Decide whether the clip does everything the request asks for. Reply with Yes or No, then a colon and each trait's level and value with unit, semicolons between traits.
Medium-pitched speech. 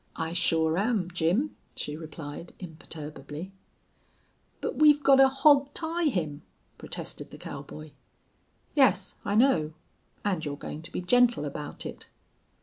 Yes: medium, 180 Hz